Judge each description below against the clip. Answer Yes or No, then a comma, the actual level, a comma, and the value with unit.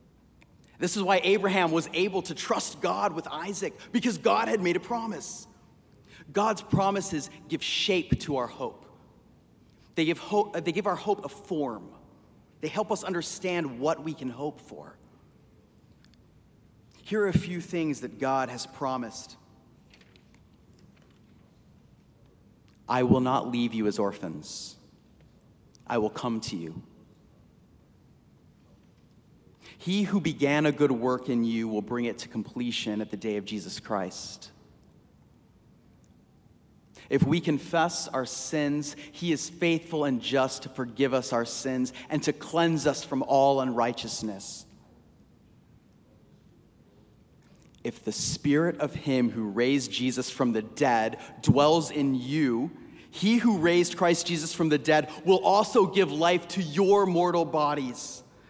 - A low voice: No, medium, 150 Hz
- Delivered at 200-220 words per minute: No, slow, 135 wpm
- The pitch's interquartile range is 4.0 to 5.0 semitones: No, wide, 5.5 semitones